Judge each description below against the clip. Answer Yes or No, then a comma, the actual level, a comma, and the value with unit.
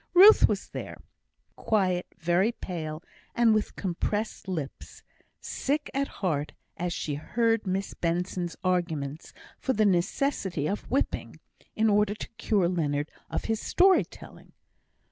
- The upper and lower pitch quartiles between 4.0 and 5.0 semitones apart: Yes, average, 4.6 semitones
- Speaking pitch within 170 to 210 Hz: Yes, high, 190 Hz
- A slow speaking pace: Yes, slow, 130 wpm